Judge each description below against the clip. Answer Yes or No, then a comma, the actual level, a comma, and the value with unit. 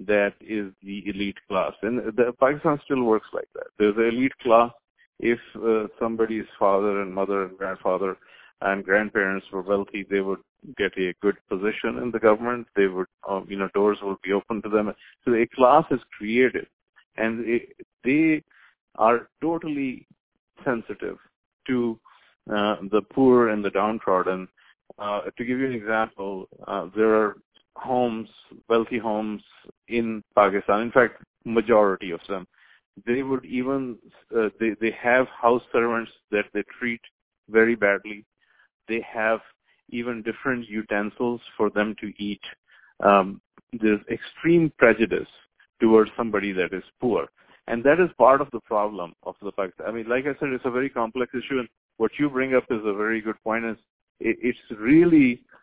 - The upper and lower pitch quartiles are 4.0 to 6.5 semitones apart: No, average, 3.2 semitones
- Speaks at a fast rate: No, average, 165 wpm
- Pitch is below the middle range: Yes, low, 115 Hz